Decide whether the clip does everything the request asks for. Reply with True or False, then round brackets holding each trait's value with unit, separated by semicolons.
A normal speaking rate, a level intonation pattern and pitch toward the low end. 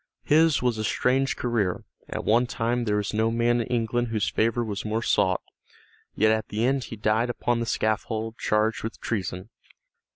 True (185 wpm; 1.9 semitones; 115 Hz)